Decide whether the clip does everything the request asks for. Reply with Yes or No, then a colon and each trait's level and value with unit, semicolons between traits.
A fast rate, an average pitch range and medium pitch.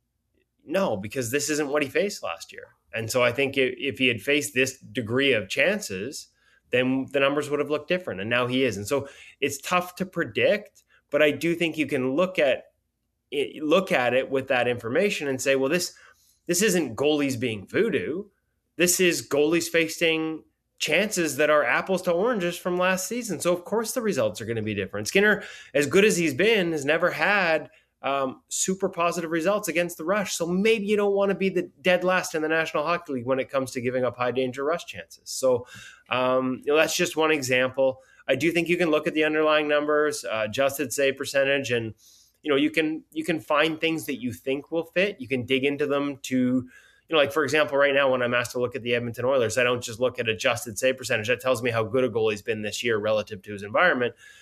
Yes: fast, 225 wpm; average, 5.0 semitones; medium, 145 Hz